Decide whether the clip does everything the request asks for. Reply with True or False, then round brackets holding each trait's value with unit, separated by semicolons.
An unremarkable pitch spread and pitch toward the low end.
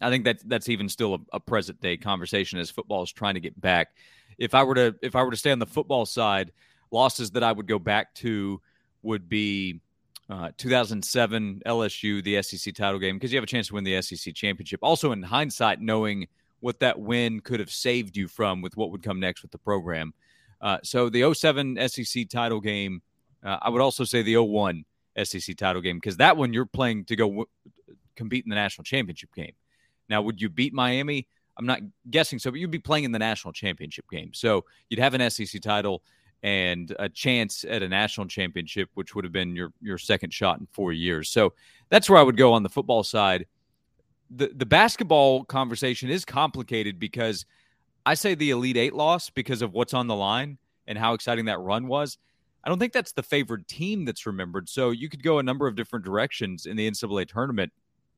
True (4.4 semitones; 115 Hz)